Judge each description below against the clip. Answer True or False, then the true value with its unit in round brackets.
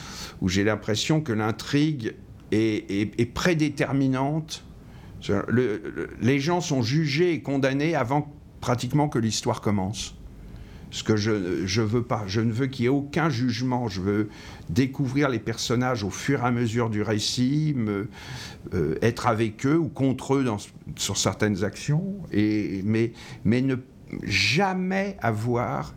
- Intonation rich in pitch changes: False (4.8 semitones)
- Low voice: True (120 Hz)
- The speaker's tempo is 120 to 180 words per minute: True (155 wpm)